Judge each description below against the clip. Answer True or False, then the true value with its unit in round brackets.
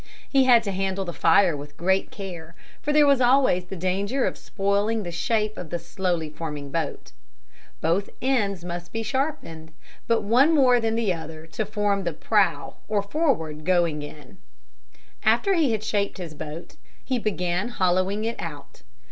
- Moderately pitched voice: False (195 Hz)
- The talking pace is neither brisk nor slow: True (170 wpm)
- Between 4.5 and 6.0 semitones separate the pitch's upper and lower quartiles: True (5.2 semitones)